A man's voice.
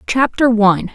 No: female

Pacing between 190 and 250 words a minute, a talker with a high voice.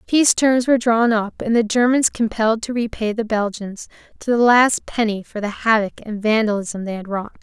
Yes: average, 200 wpm; high, 225 Hz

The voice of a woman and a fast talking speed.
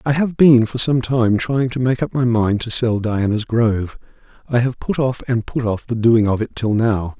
No: male; fast, 240 wpm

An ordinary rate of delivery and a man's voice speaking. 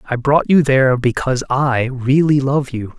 Yes: average, 180 wpm; male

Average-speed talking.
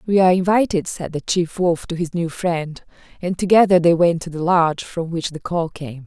No: fast, 230 wpm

